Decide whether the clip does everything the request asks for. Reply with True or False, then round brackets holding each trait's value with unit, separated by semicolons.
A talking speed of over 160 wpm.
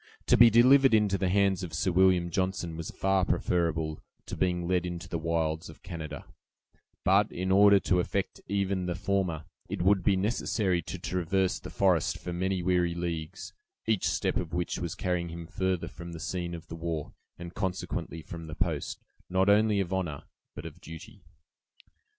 True (180 wpm)